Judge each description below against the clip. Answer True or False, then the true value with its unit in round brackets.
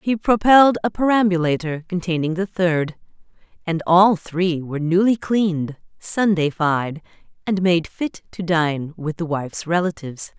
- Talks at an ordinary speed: False (125 wpm)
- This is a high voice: False (175 Hz)